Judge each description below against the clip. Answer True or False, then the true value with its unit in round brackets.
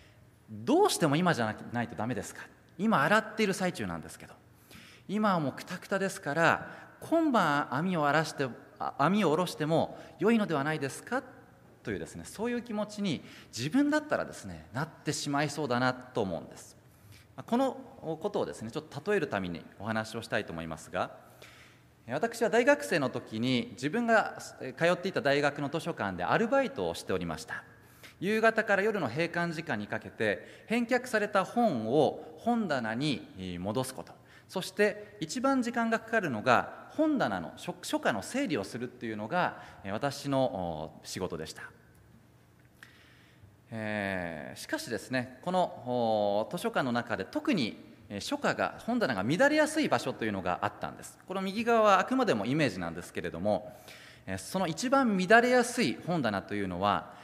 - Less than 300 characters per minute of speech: False (330 characters per minute)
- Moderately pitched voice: True (155 Hz)